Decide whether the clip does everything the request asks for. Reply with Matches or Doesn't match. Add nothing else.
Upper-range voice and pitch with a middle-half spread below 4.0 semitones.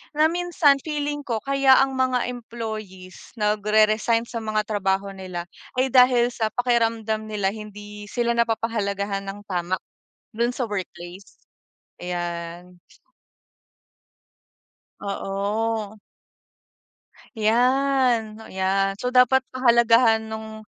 Matches